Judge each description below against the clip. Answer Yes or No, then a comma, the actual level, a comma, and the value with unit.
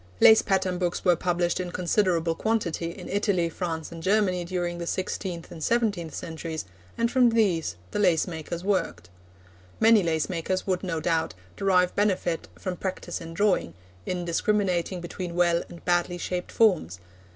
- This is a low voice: No, medium, 180 Hz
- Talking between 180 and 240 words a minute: No, average, 160 wpm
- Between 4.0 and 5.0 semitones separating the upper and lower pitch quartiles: No, narrow, 2.4 semitones